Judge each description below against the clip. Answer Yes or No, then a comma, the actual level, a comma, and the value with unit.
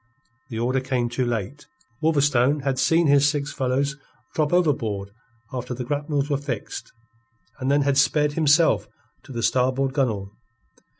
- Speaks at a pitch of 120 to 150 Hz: Yes, low, 135 Hz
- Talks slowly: No, average, 145 wpm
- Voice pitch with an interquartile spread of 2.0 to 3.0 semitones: Yes, average, 2.7 semitones